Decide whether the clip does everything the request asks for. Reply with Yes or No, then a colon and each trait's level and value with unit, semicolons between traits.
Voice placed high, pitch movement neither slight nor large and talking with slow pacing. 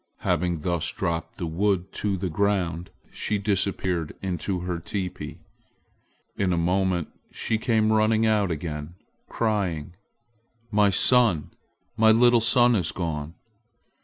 No: very low, 95 Hz; average, 4.1 semitones; slow, 125 wpm